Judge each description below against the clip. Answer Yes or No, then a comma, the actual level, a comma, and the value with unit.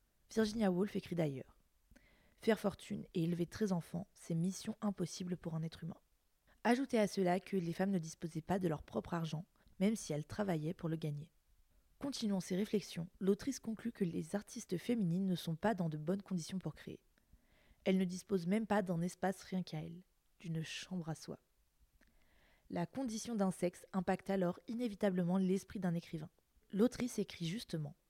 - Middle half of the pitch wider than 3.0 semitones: Yes, average, 3.4 semitones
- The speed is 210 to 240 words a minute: No, average, 175 wpm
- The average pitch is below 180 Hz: No, medium, 185 Hz